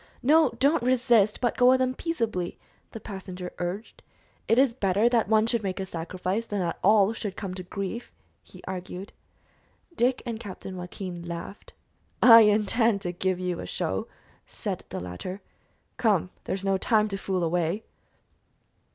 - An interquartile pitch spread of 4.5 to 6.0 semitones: No, average, 3.9 semitones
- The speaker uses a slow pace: No, average, 165 wpm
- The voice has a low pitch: No, high, 200 Hz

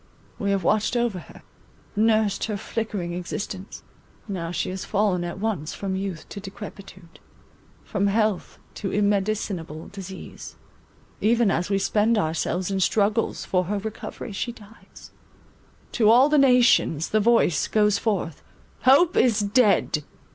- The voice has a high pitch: Yes, high, 200 Hz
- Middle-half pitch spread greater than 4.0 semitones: No, narrow, 2.6 semitones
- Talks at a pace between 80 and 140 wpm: Yes, slow, 135 wpm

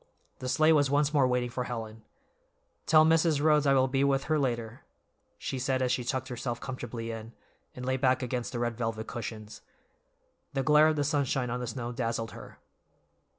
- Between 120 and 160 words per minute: No, average, 195 wpm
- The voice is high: No, low, 130 Hz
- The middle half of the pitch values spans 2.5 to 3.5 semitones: Yes, average, 2.9 semitones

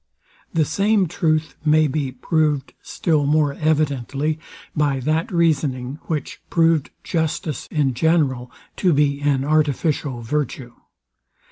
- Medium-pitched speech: Yes, medium, 150 Hz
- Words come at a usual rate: No, slow, 115 wpm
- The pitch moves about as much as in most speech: No, narrow, 2.3 semitones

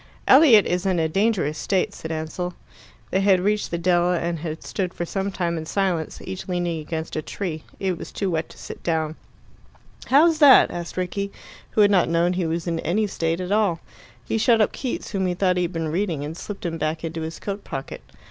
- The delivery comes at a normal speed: No, fast, 220 wpm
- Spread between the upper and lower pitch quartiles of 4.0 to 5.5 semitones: No, average, 3.2 semitones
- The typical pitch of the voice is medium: Yes, medium, 180 Hz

